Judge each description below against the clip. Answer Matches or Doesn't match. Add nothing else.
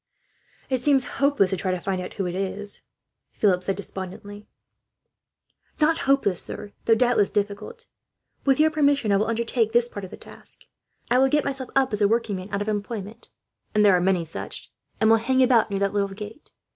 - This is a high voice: Matches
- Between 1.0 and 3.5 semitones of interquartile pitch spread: Doesn't match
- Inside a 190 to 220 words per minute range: Matches